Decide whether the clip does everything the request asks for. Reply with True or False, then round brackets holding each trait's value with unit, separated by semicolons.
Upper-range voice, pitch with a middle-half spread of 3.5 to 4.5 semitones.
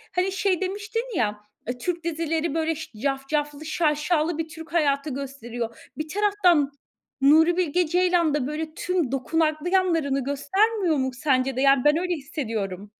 True (310 Hz; 4.2 semitones)